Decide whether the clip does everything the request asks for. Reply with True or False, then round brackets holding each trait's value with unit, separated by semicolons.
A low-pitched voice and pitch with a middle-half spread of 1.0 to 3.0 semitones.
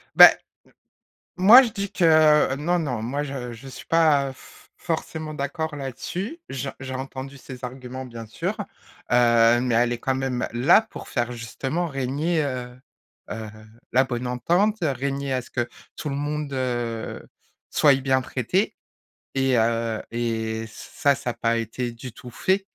False (130 Hz; 3.6 semitones)